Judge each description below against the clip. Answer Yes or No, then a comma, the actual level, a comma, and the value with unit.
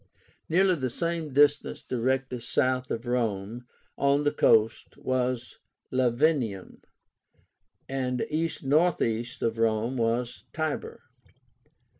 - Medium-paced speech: No, slow, 100 wpm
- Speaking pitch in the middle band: No, low, 130 Hz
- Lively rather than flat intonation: No, average, 3.9 semitones